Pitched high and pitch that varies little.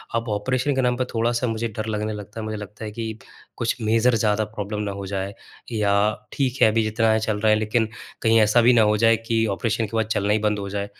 No: low, 110 Hz; narrow, 1.5 semitones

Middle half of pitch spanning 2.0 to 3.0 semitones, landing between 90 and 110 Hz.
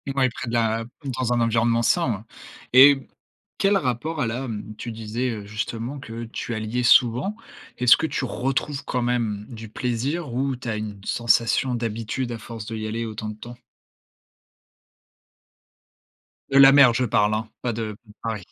No: narrow, 2.5 semitones; low, 120 Hz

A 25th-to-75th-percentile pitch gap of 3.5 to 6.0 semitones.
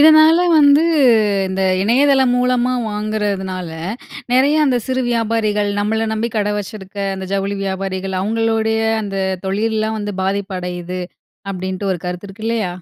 No: average, 3.1 semitones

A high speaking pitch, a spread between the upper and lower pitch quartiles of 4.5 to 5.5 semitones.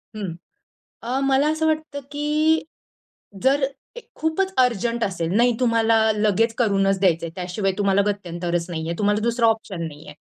Yes: high, 210 Hz; average, 5.2 semitones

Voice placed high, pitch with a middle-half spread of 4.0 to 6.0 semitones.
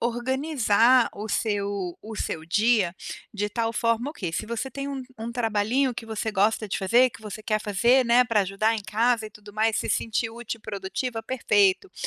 No: high, 225 Hz; narrow, 2.6 semitones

